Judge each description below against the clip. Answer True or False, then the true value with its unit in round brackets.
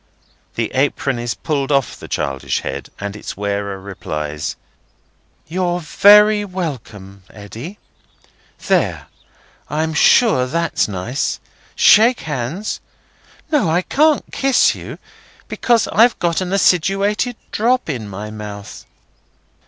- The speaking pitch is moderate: True (150 Hz)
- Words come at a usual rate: False (115 wpm)